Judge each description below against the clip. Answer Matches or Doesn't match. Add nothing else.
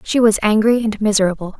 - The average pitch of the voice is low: Doesn't match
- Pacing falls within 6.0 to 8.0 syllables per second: Matches